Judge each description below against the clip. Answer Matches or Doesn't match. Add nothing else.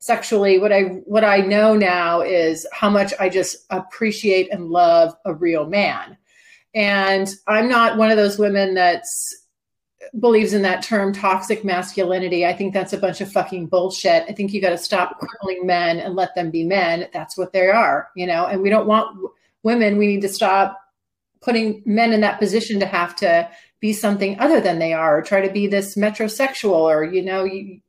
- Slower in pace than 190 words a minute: Doesn't match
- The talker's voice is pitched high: Matches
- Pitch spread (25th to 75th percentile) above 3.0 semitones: Doesn't match